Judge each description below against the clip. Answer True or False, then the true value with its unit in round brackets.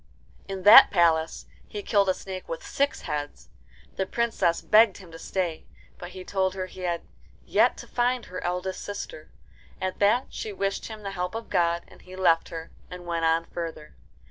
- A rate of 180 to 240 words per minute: True (190 wpm)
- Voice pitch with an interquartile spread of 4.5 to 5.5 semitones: False (3.0 semitones)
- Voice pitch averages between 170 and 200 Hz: True (185 Hz)